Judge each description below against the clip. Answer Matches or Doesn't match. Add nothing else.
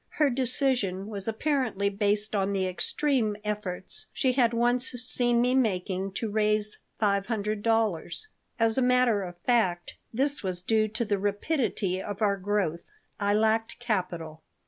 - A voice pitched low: Doesn't match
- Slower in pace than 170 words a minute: Matches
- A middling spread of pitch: Matches